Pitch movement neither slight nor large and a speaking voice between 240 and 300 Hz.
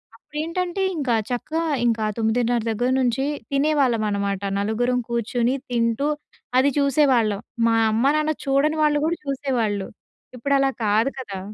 Yes: average, 4.0 semitones; very high, 250 Hz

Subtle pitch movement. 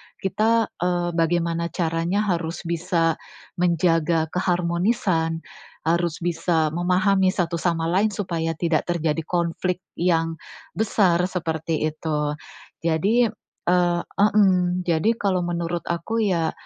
Yes: narrow, 1.8 semitones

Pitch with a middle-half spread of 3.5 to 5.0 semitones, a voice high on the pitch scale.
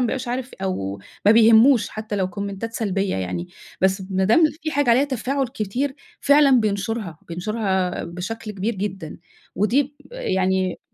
Yes: average, 4.6 semitones; high, 215 Hz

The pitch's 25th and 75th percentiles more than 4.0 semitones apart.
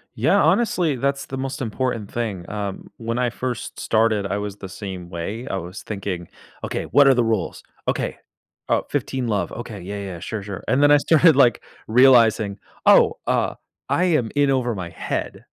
Yes: average, 4.7 semitones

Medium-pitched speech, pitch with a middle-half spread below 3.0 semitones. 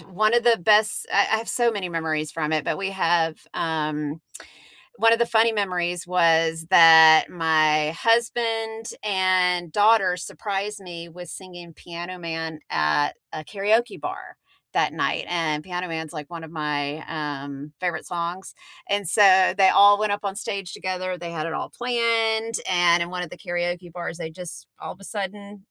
No: medium, 180 Hz; average, 3.9 semitones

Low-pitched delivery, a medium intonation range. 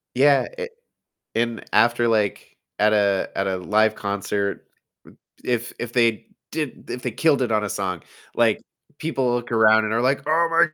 Yes: low, 115 Hz; average, 3.6 semitones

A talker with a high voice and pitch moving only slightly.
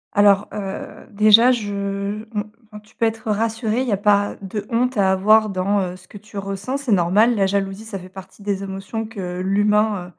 Yes: high, 205 Hz; narrow, 2.1 semitones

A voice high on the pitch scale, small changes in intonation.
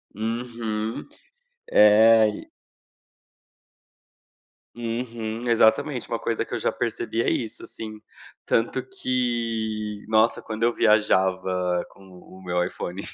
No: low, 110 Hz; narrow, 1.8 semitones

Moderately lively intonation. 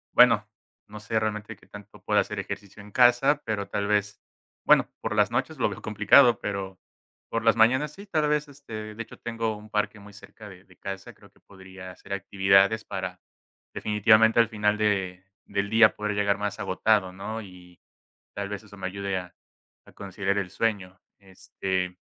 No: narrow, 2.3 semitones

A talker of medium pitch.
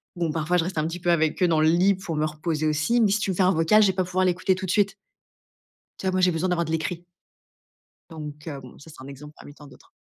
Yes: medium, 170 Hz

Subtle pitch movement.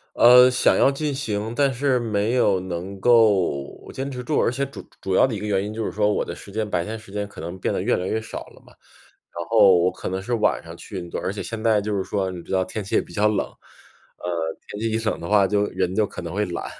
No: average, 3.3 semitones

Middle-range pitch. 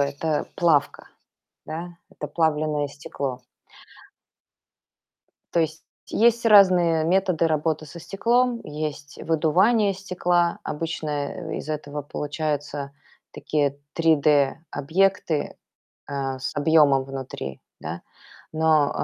Yes: medium, 155 Hz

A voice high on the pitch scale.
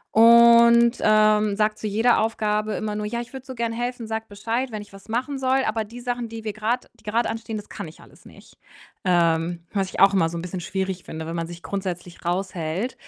Yes: high, 215 Hz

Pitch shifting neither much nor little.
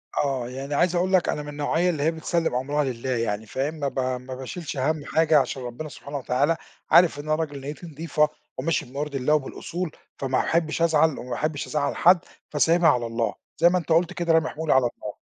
Yes: average, 3.5 semitones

